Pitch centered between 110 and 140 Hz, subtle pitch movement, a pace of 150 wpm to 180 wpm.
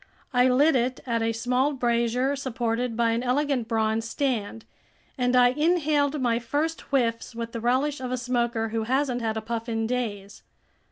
No: high, 245 Hz; narrow, 2.3 semitones; average, 175 wpm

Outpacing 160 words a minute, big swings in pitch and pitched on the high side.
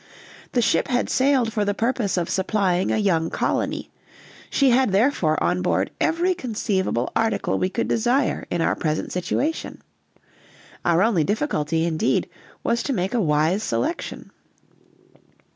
No: average, 145 wpm; wide, 5.8 semitones; high, 205 Hz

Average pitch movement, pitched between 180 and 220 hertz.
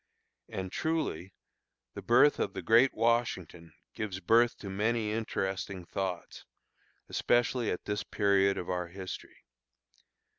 No: average, 3.8 semitones; low, 100 Hz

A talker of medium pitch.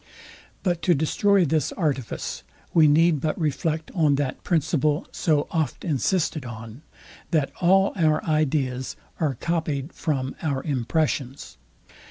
Yes: medium, 155 Hz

